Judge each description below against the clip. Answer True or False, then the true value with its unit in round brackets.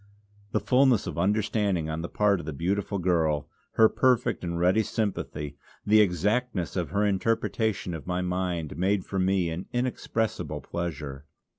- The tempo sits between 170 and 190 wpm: False (155 wpm)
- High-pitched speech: False (95 Hz)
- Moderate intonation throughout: True (3.9 semitones)